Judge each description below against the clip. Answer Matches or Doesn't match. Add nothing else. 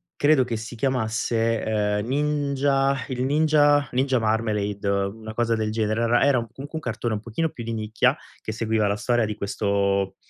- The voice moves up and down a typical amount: Matches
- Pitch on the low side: Matches